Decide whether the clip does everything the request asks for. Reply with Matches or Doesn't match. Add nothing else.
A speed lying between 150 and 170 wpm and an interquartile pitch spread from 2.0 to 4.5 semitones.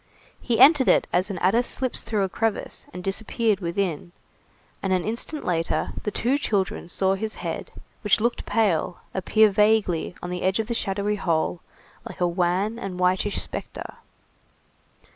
Matches